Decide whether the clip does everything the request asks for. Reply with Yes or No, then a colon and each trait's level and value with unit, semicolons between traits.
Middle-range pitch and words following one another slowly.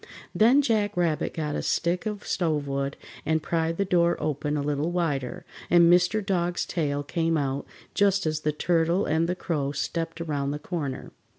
No: medium, 165 Hz; average, 175 wpm